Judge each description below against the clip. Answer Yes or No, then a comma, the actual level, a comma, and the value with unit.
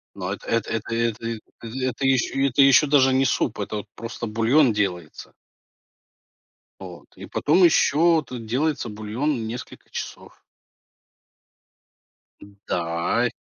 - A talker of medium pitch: No, low, 120 Hz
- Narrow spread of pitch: No, average, 3.8 semitones